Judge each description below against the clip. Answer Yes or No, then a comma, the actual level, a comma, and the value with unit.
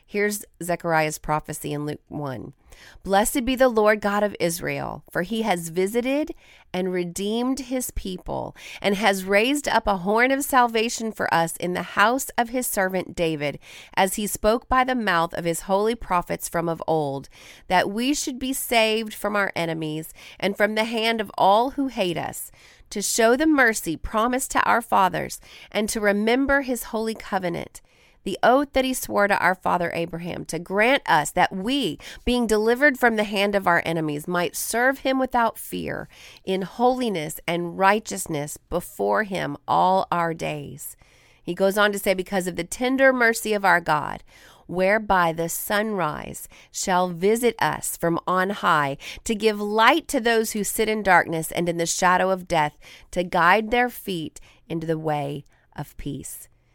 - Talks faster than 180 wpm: No, average, 175 wpm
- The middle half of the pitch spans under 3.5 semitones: No, average, 5.2 semitones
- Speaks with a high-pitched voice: Yes, high, 200 Hz